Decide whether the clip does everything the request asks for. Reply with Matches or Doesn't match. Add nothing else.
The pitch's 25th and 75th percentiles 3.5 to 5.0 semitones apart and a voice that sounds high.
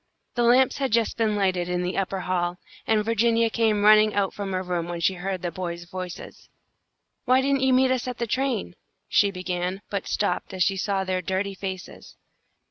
Matches